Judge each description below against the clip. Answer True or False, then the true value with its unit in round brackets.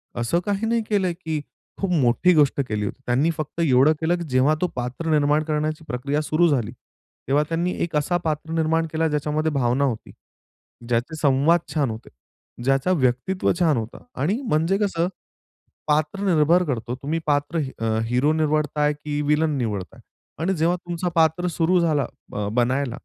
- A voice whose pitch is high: False (150 Hz)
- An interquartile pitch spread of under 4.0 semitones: True (3.6 semitones)